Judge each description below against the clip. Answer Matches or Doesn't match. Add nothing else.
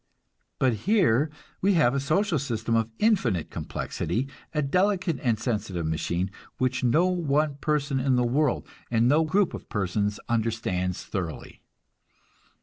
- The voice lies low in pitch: Matches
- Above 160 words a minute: Doesn't match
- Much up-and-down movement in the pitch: Matches